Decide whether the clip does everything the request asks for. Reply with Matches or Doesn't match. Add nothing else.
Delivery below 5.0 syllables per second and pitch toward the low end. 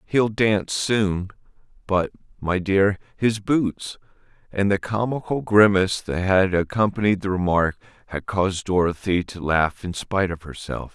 Matches